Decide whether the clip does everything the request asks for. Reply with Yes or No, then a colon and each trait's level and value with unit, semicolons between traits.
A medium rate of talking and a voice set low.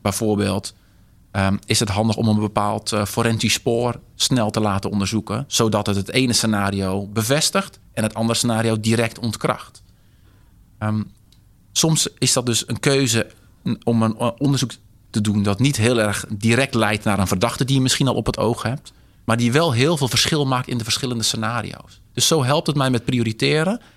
Yes: average, 185 wpm; low, 115 Hz